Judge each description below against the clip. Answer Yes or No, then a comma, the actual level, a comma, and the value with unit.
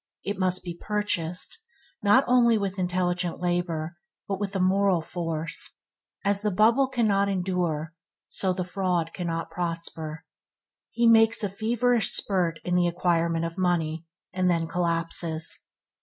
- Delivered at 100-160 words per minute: Yes, slow, 135 wpm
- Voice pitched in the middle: Yes, medium, 180 Hz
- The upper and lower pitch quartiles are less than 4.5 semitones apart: Yes, average, 3.1 semitones